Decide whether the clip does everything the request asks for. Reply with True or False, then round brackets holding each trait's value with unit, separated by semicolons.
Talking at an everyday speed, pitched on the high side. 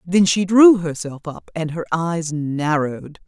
False (165 wpm; 165 Hz)